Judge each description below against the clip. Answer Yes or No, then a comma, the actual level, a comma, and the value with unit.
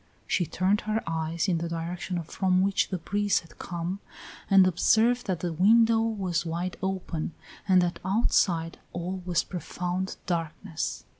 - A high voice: No, medium, 180 Hz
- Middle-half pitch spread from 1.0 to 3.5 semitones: Yes, narrow, 2.6 semitones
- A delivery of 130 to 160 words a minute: Yes, average, 150 wpm